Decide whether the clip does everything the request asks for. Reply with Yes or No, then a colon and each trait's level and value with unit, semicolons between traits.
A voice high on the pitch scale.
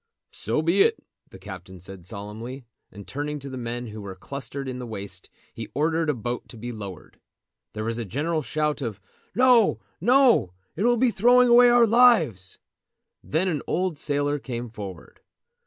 No: low, 135 Hz